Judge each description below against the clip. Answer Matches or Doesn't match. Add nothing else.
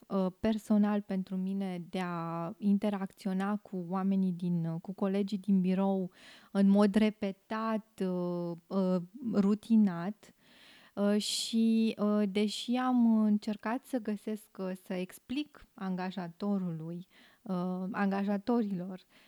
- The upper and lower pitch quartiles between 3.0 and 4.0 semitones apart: Doesn't match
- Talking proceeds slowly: Matches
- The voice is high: Matches